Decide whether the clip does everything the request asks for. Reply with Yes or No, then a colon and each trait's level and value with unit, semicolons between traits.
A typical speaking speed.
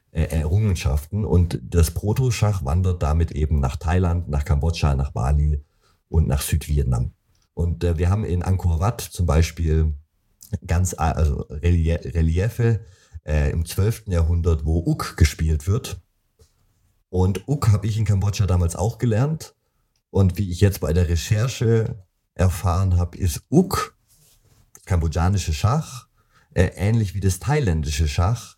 Yes: average, 135 wpm